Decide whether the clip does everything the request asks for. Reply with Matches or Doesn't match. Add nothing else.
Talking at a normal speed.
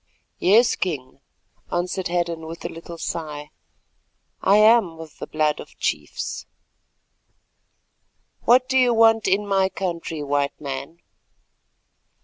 Doesn't match